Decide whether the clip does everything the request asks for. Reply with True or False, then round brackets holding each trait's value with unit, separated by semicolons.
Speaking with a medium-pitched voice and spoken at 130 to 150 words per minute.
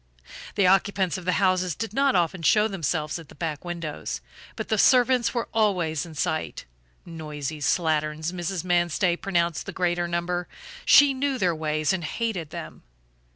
False (175 Hz; 160 wpm)